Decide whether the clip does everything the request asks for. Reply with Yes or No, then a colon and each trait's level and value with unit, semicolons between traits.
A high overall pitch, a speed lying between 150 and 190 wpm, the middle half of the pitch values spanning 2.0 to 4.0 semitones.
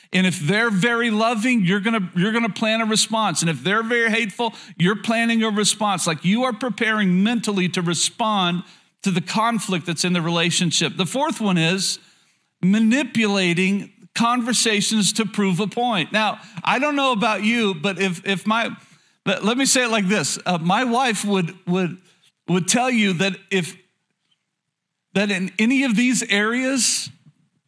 Yes: high, 200 Hz; average, 175 wpm; average, 3.7 semitones